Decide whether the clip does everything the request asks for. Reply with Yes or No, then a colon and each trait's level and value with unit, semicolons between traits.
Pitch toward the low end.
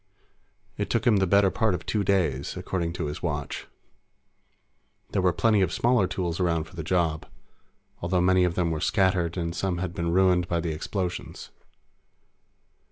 Yes: very low, 90 Hz